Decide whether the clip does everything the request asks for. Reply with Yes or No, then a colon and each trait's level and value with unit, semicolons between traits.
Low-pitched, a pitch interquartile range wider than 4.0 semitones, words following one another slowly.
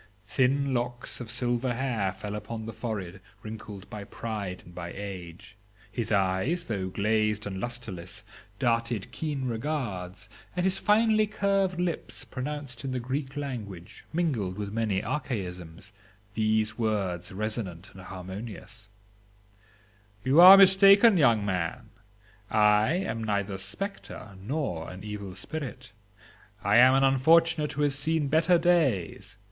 Yes: low, 110 Hz; wide, 5.5 semitones; slow, 130 wpm